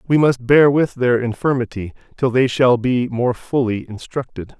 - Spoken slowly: No, average, 170 wpm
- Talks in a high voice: No, low, 125 Hz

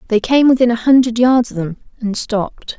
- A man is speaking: No, female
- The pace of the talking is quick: Yes, fast, 215 wpm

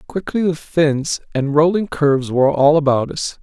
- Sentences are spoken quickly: No, average, 175 wpm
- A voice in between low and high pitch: Yes, medium, 150 Hz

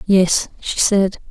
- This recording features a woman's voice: Yes, female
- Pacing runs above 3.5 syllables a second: No, 2.9 syllables/s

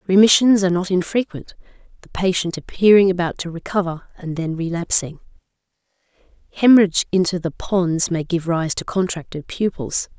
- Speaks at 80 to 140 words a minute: Yes, slow, 135 wpm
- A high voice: No, medium, 180 Hz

